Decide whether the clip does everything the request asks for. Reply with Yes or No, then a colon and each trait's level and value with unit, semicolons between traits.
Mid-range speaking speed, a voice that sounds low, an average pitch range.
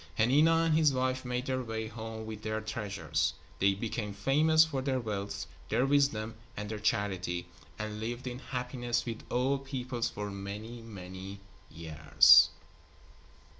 Yes: average, 145 wpm; low, 115 Hz; average, 4.2 semitones